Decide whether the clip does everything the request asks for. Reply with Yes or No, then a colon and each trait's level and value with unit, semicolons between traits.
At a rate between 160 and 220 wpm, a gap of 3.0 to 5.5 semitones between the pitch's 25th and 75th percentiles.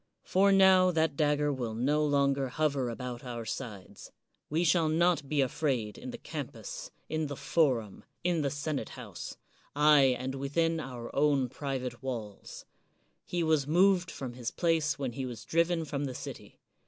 Yes: average, 165 wpm; average, 4.1 semitones